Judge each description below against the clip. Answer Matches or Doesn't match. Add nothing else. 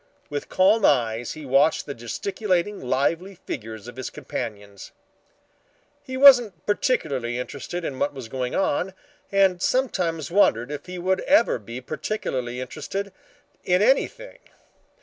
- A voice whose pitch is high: Doesn't match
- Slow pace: Matches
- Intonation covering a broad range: Matches